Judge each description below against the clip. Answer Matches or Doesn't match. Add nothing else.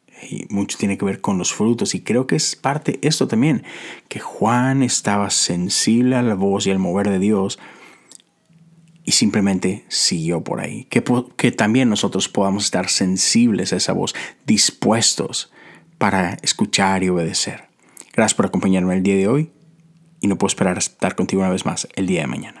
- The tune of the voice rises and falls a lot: Matches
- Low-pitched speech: Matches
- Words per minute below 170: Doesn't match